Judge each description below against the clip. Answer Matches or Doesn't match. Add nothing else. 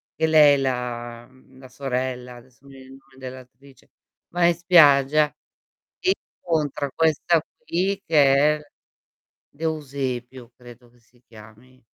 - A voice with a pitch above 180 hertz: Doesn't match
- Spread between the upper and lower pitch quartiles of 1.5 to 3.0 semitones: Doesn't match